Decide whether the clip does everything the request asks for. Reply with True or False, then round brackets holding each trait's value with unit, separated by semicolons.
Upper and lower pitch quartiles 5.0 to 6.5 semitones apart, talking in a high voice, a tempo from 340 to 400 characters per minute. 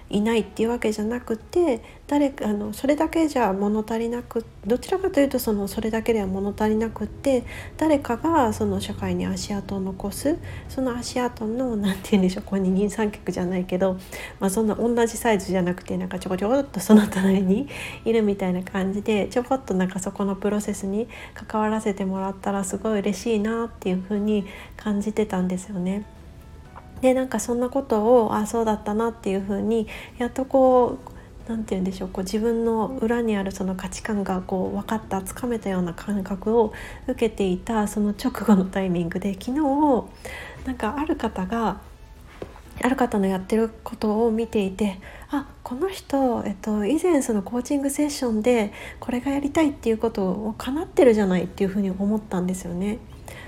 False (3.5 semitones; 215 Hz; 390 characters per minute)